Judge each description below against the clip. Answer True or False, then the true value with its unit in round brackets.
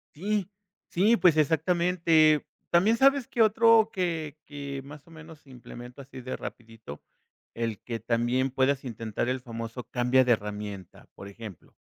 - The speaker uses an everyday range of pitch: False (6.6 semitones)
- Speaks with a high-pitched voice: False (135 Hz)